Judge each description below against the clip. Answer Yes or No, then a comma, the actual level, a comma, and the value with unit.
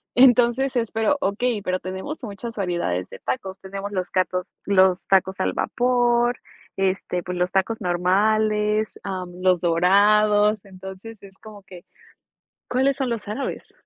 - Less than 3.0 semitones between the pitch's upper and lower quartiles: No, average, 3.5 semitones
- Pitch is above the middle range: Yes, high, 200 Hz